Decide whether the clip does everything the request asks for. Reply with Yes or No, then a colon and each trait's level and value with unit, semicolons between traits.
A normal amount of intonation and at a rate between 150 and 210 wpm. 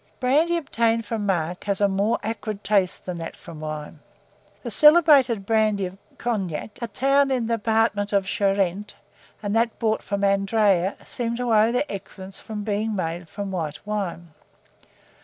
Yes: average, 3.1 semitones; average, 160 wpm